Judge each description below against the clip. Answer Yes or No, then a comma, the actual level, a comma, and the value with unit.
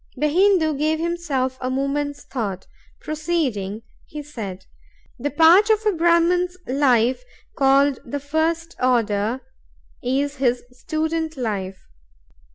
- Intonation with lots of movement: No, average, 4.5 semitones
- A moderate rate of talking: No, slow, 115 wpm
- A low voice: No, very high, 285 Hz